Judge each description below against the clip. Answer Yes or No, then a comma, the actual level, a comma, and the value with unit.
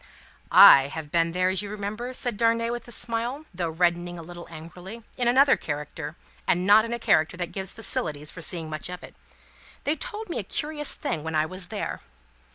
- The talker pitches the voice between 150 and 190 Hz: Yes, medium, 185 Hz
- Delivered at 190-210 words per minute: Yes, fast, 205 wpm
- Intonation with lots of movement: Yes, wide, 5.9 semitones